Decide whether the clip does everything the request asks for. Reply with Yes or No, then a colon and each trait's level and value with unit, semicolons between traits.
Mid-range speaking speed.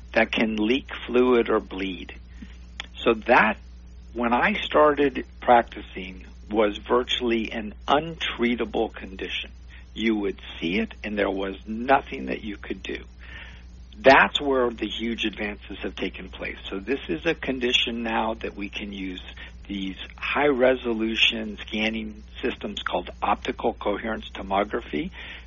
No: slow, 130 wpm